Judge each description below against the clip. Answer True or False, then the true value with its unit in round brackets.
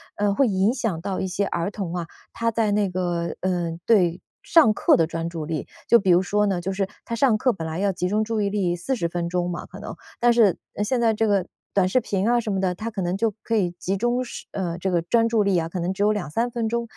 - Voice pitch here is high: True (195 Hz)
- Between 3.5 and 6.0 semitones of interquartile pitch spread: True (4.2 semitones)